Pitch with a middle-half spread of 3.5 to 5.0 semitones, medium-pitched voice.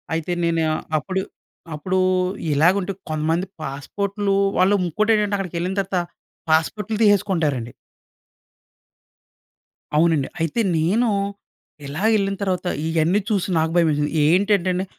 Yes: average, 3.8 semitones; medium, 180 Hz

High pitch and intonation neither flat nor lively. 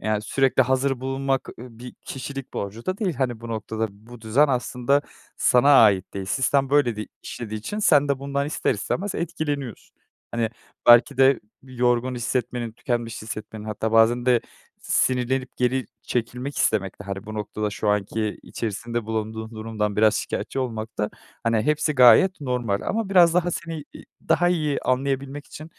No: low, 125 Hz; average, 3.9 semitones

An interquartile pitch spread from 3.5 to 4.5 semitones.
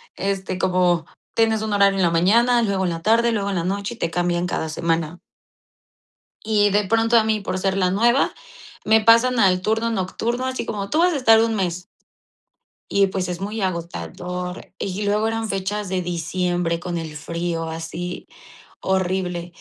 Yes: average, 3.8 semitones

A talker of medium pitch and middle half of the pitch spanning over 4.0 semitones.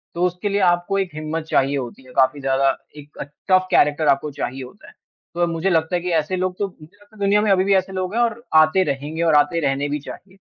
Yes: medium, 165 Hz; average, 4.5 semitones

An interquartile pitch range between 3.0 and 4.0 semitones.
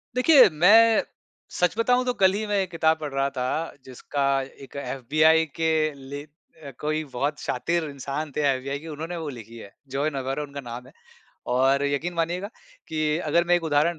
Yes: average, 3.7 semitones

